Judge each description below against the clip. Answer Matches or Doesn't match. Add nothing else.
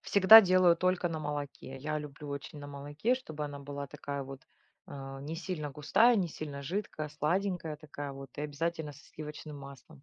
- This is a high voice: Doesn't match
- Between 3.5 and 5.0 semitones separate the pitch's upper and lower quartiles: Doesn't match